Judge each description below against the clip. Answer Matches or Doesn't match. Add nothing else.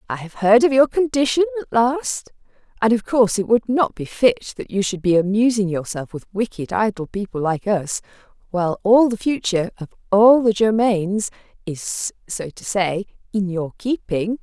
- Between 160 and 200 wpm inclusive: Matches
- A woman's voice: Matches